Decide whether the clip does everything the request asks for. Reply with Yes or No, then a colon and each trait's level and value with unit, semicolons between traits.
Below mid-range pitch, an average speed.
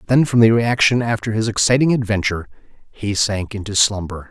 Yes: low, 110 Hz; average, 165 wpm